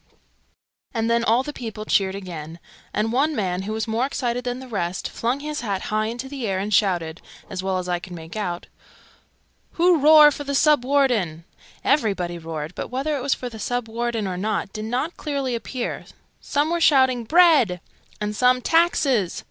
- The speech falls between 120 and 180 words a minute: No, average, 190 wpm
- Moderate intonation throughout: No, wide, 5.9 semitones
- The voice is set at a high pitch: Yes, high, 230 Hz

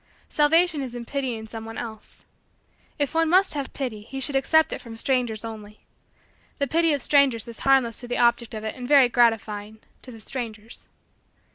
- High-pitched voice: Yes, high, 245 Hz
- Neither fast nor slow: Yes, average, 180 wpm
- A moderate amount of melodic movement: Yes, average, 3.9 semitones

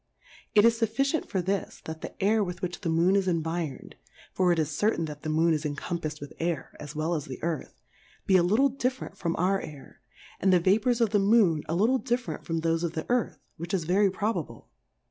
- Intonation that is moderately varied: Yes, average, 4.4 semitones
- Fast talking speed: Yes, fast, 225 wpm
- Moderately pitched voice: Yes, medium, 180 Hz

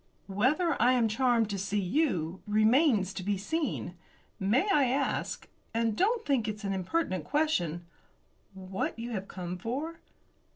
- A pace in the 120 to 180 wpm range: Yes, average, 150 wpm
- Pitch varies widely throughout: Yes, wide, 6.5 semitones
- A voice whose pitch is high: Yes, high, 220 Hz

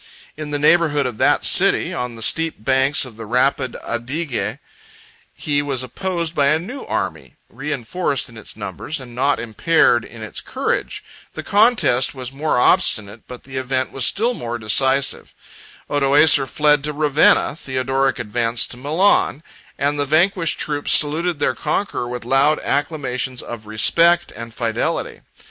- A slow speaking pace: No, average, 155 wpm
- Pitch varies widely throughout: No, average, 3.9 semitones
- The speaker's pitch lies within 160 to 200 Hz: No, medium, 140 Hz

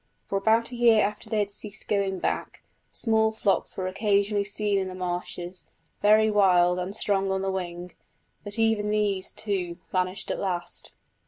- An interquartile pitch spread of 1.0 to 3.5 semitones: Yes, narrow, 2.4 semitones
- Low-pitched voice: No, high, 200 Hz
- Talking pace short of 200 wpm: Yes, average, 170 wpm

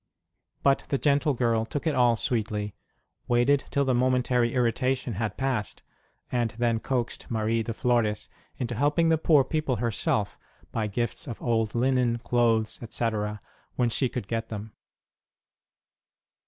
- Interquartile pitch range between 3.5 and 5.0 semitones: No, narrow, 2.5 semitones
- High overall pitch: No, low, 120 Hz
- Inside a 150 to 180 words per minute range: No, average, 140 wpm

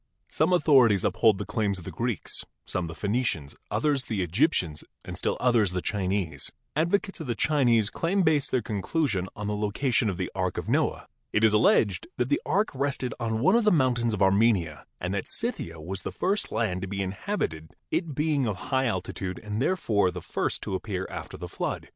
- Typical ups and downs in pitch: No, wide, 6.5 semitones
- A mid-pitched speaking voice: No, low, 110 Hz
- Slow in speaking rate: No, average, 200 wpm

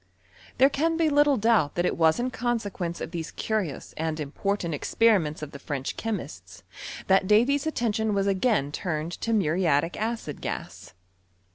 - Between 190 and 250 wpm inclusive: No, average, 155 wpm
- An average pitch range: No, wide, 6.4 semitones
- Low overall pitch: No, high, 200 Hz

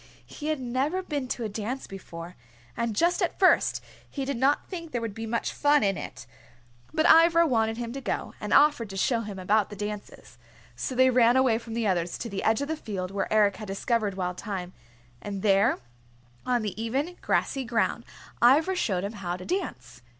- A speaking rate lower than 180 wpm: No, fast, 205 wpm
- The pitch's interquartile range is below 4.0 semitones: No, average, 5.3 semitones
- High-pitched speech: Yes, high, 230 Hz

